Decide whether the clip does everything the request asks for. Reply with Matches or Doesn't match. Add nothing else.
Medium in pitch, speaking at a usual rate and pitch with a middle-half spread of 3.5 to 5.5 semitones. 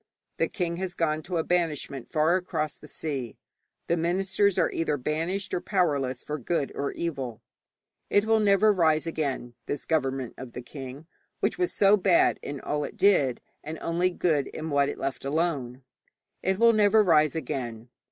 Matches